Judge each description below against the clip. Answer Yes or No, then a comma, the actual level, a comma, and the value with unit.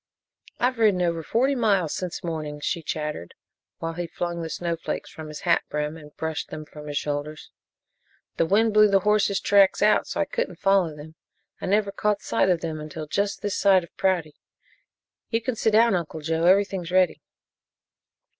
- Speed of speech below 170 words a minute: No, average, 185 wpm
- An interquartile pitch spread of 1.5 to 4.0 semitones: No, average, 4.4 semitones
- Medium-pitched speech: Yes, medium, 175 Hz